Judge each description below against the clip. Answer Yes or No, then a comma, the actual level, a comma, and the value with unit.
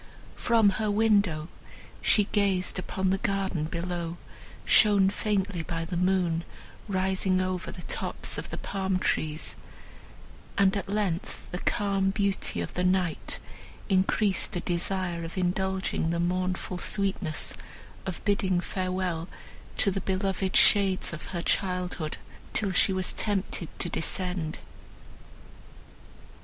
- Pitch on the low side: No, medium, 185 Hz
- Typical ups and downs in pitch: No, narrow, 1.9 semitones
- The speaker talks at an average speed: No, slow, 125 wpm